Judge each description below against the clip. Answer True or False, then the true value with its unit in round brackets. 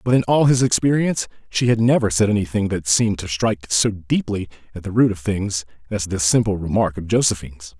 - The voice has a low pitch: True (100 Hz)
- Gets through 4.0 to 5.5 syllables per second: False (5.9 syllables/s)